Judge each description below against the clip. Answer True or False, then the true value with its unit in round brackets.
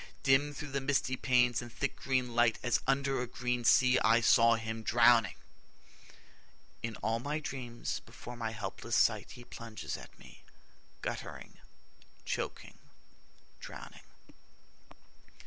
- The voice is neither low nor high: False (120 Hz)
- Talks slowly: True (130 wpm)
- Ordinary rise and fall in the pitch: False (2.2 semitones)